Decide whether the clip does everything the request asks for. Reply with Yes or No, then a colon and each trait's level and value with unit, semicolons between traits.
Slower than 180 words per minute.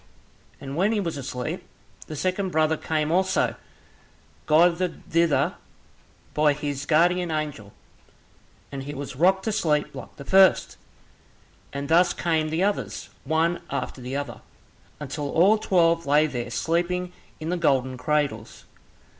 Yes: average, 140 wpm